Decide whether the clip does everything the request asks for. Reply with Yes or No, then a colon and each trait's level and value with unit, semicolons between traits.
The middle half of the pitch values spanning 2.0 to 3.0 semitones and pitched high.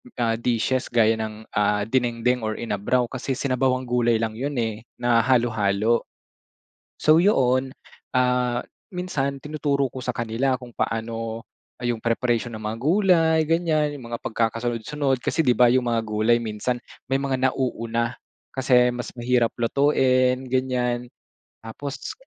No: narrow, 2.4 semitones; low, 125 Hz